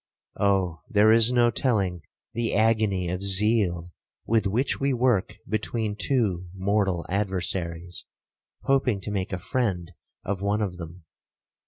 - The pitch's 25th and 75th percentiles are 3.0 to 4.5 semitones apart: Yes, average, 3.6 semitones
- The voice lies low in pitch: Yes, low, 100 Hz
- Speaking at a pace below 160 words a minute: Yes, slow, 135 wpm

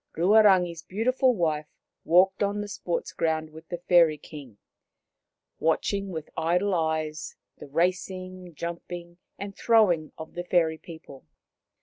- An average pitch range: Yes, average, 3.0 semitones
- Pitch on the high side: No, medium, 175 Hz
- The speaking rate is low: Yes, slow, 130 wpm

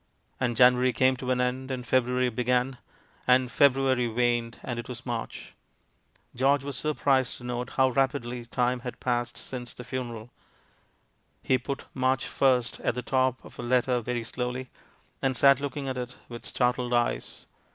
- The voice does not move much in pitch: Yes, narrow, 1.3 semitones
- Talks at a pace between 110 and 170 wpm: Yes, average, 165 wpm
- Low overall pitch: Yes, low, 125 Hz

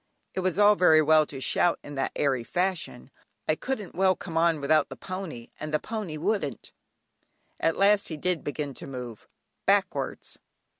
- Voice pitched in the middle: Yes, medium, 160 Hz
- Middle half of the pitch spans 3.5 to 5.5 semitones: Yes, average, 4.5 semitones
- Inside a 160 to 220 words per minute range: Yes, average, 170 wpm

